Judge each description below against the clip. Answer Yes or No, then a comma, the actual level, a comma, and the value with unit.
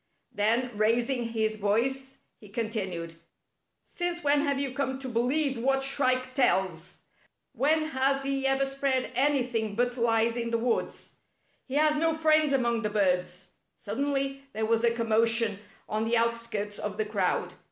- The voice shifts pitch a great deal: No, average, 3.8 semitones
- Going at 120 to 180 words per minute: Yes, average, 170 wpm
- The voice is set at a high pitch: Yes, high, 240 Hz